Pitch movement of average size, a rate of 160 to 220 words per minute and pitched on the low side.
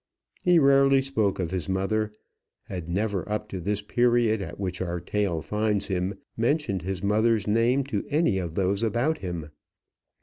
Yes: average, 3.9 semitones; average, 165 wpm; low, 105 Hz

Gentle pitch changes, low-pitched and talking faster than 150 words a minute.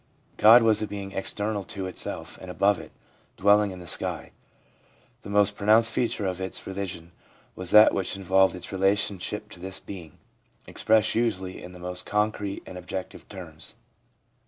Yes: narrow, 2.2 semitones; very low, 95 Hz; average, 165 wpm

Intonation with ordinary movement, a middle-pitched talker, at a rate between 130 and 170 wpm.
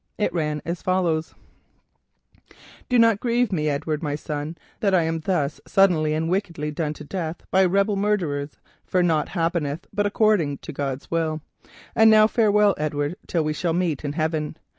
Yes: average, 4.3 semitones; medium, 165 Hz; average, 165 wpm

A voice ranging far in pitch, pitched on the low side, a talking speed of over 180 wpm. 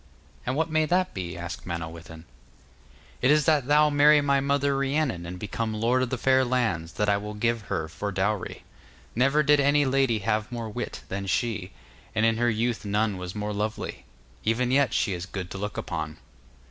Yes: wide, 5.8 semitones; low, 115 Hz; average, 195 wpm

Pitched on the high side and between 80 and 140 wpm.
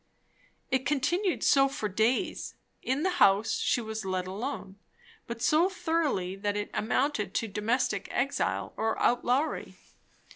Yes: high, 235 Hz; slow, 135 wpm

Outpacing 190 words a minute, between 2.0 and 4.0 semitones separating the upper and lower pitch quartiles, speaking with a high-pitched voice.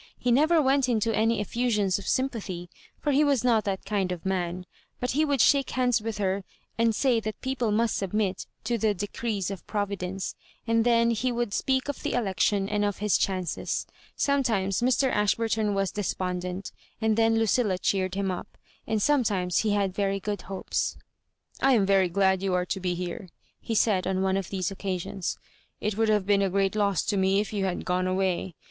Yes: fast, 205 wpm; average, 3.2 semitones; high, 205 Hz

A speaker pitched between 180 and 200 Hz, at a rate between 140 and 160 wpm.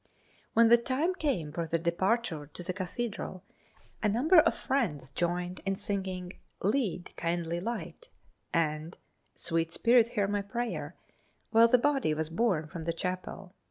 Yes: high, 190 Hz; average, 155 wpm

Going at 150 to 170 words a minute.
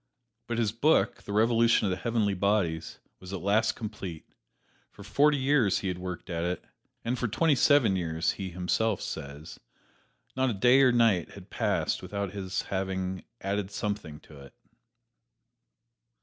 Yes: average, 165 wpm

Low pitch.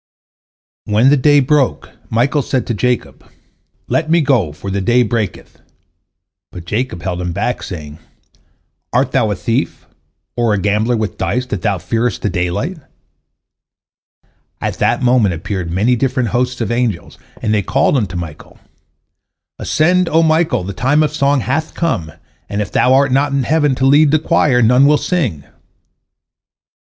Yes: low, 125 Hz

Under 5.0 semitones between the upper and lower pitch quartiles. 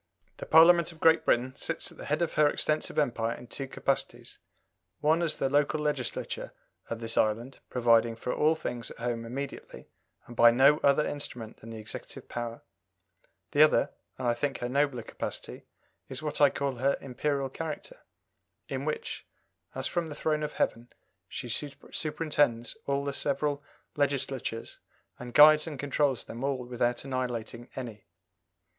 Yes: average, 3.8 semitones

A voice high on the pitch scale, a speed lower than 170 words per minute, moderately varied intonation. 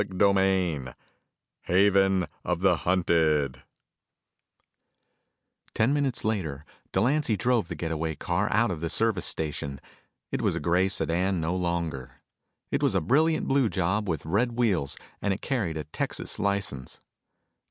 No: very low, 95 Hz; average, 140 wpm; average, 4.3 semitones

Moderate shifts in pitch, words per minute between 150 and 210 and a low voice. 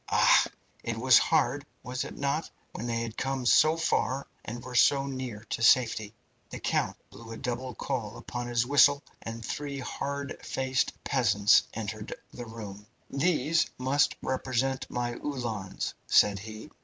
Yes: average, 3.2 semitones; average, 155 wpm; low, 125 Hz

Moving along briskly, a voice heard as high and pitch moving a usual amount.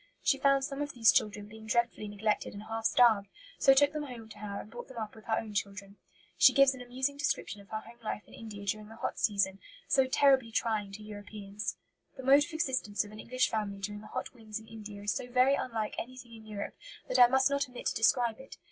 Yes: fast, 240 wpm; high, 225 Hz; average, 3.8 semitones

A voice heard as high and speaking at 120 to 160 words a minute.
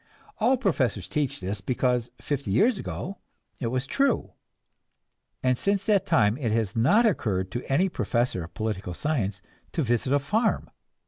No: low, 125 Hz; average, 155 wpm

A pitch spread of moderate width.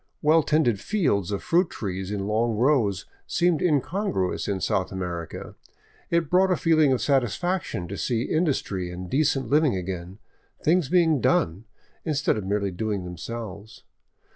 No: wide, 8.5 semitones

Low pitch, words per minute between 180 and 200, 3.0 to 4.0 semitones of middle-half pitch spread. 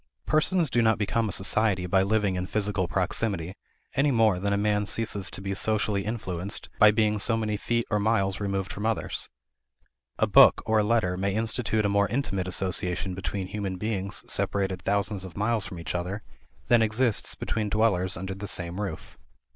No: low, 100 Hz; average, 185 wpm; narrow, 2.4 semitones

